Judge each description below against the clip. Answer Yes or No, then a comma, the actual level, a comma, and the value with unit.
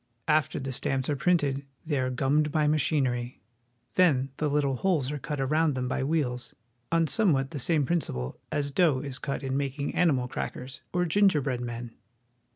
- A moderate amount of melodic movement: Yes, average, 3.0 semitones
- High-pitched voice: No, medium, 140 Hz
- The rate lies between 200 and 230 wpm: No, average, 170 wpm